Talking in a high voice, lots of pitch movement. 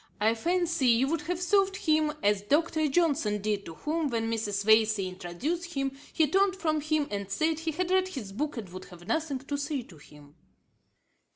Yes: very high, 280 Hz; wide, 7.7 semitones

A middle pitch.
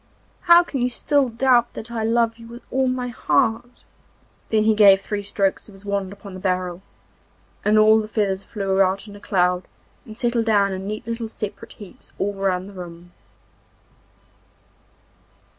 No: high, 215 Hz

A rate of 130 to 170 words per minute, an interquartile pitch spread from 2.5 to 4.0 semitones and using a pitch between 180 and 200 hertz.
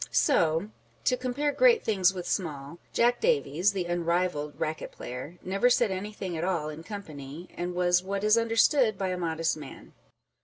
No: average, 165 wpm; average, 4.7 semitones; medium, 185 Hz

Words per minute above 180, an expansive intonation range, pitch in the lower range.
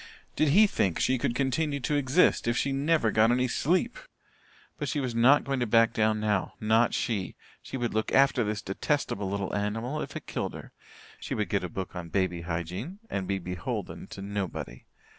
Yes: average, 200 wpm; wide, 5.7 semitones; low, 115 Hz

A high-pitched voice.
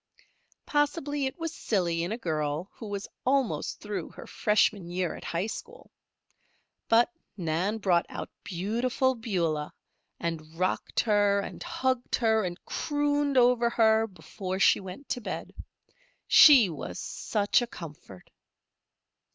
Yes: high, 210 Hz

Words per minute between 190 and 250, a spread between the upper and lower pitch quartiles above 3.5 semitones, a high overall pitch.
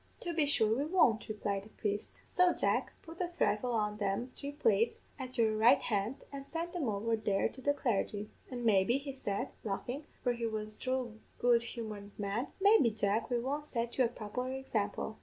Yes: average, 200 wpm; average, 4.2 semitones; high, 235 Hz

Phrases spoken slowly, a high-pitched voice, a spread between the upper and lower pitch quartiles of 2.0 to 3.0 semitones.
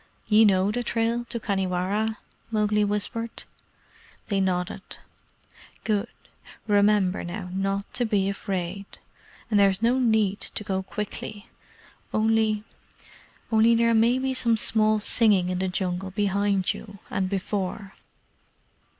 Yes: slow, 125 wpm; high, 205 Hz; narrow, 2.6 semitones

